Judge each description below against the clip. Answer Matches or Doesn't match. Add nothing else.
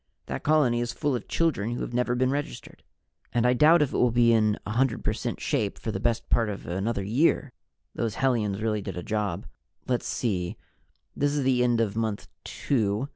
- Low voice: Matches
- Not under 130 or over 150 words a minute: Doesn't match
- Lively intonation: Doesn't match